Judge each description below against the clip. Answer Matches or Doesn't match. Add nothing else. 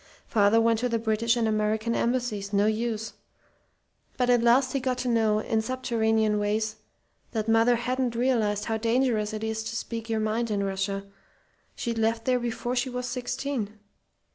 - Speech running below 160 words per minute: Doesn't match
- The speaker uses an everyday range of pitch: Doesn't match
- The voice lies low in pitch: Doesn't match